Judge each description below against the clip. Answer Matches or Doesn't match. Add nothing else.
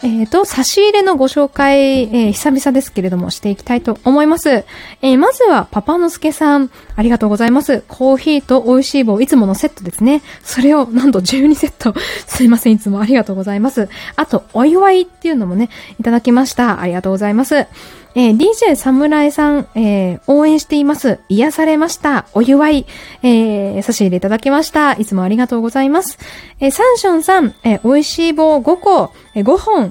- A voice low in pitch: Doesn't match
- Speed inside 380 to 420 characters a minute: Matches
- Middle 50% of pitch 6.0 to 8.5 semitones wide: Doesn't match